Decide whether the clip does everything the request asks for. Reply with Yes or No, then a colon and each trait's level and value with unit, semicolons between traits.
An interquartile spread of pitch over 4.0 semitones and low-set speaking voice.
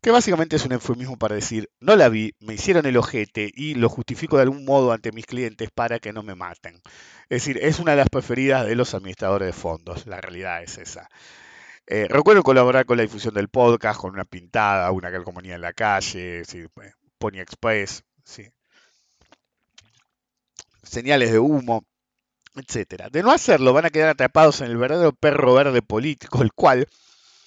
Yes: average, 4.6 semitones; low, 115 Hz